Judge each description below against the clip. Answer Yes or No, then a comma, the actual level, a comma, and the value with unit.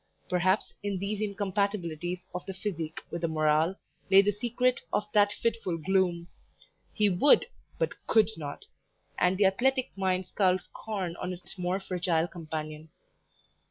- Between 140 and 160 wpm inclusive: Yes, average, 145 wpm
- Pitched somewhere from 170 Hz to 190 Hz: Yes, medium, 185 Hz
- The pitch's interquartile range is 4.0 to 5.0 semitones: No, average, 3.2 semitones